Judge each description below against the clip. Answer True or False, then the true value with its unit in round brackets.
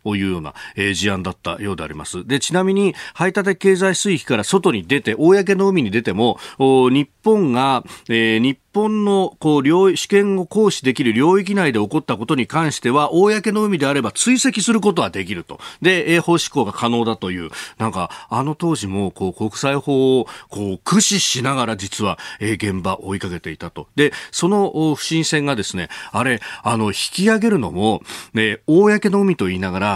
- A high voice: False (140 Hz)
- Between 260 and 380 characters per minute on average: True (345 characters per minute)